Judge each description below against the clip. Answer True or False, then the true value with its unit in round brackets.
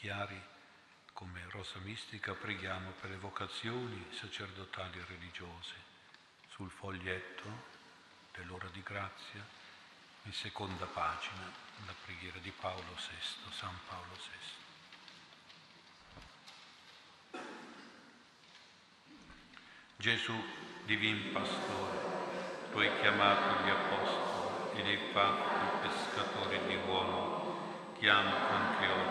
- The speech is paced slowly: True (95 wpm)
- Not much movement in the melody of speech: True (1.9 semitones)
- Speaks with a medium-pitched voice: False (95 Hz)